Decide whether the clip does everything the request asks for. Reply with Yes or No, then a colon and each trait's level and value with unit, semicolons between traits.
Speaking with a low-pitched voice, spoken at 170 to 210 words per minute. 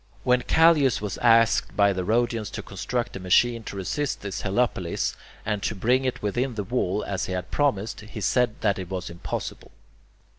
Yes: low, 110 Hz; average, 185 wpm